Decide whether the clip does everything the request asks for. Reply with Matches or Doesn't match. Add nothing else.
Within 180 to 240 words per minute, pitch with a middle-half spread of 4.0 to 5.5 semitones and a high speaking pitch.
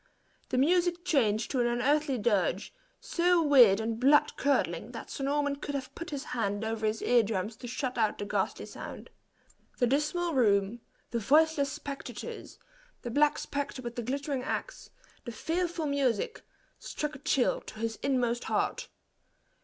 Doesn't match